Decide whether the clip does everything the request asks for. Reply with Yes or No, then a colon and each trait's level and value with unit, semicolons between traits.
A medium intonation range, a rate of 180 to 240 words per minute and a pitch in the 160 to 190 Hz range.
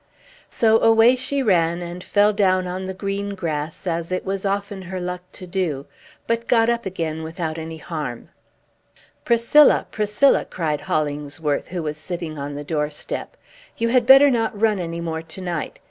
No: average, 4.6 semitones; average, 170 wpm; medium, 185 Hz